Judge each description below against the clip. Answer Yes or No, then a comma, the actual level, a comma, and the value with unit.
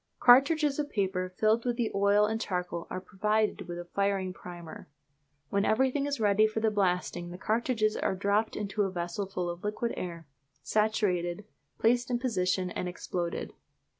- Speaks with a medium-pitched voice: No, high, 200 Hz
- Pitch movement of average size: Yes, average, 3.5 semitones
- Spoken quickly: No, average, 165 wpm